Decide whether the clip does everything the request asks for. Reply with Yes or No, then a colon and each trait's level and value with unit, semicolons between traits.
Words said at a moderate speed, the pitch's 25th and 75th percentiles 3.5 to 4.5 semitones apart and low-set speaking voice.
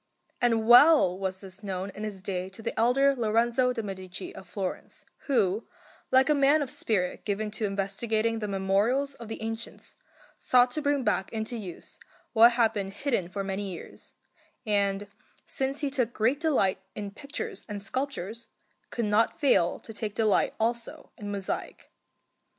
No: average, 165 wpm; average, 3.9 semitones; high, 220 Hz